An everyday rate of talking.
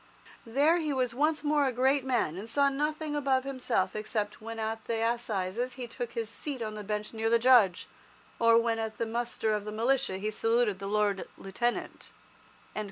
Yes: average, 190 wpm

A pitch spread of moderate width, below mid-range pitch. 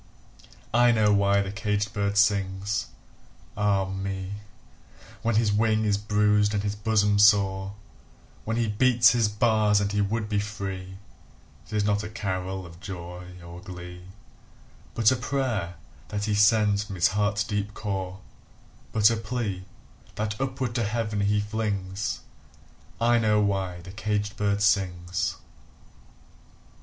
No: narrow, 1.9 semitones; low, 105 Hz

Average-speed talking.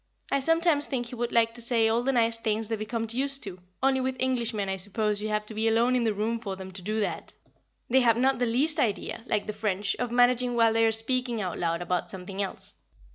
No: fast, 245 wpm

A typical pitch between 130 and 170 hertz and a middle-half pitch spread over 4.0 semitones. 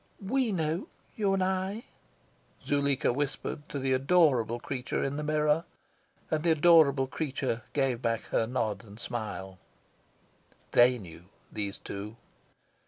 Yes: medium, 140 Hz; average, 5.3 semitones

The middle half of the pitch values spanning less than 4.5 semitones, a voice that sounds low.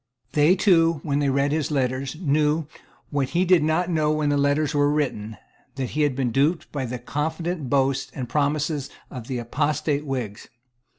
No: narrow, 2.4 semitones; medium, 145 Hz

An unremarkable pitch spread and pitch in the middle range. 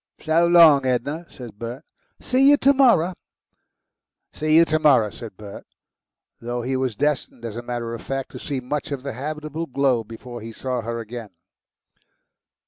No: average, 4.8 semitones; low, 130 Hz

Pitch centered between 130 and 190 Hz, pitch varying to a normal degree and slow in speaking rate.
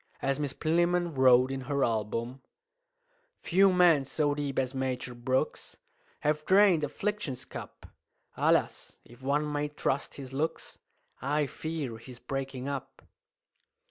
Yes: medium, 140 Hz; average, 3.0 semitones; slow, 130 wpm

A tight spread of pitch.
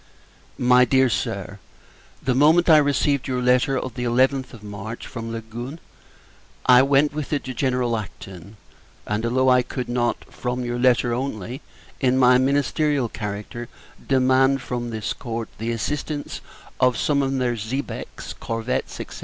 Yes: narrow, 2.3 semitones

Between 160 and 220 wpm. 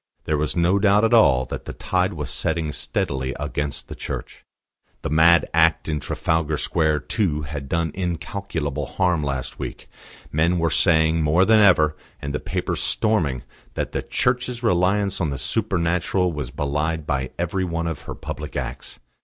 Yes: average, 170 wpm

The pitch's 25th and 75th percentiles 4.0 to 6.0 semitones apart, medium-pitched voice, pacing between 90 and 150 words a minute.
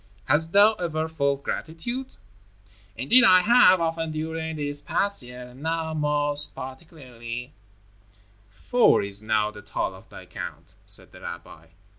Yes: average, 4.5 semitones; medium, 155 Hz; average, 140 wpm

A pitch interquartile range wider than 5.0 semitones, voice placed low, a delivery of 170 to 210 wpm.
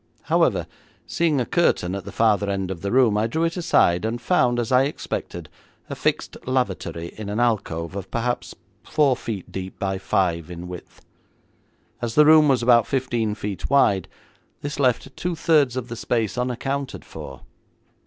Yes: wide, 5.5 semitones; low, 115 Hz; average, 175 wpm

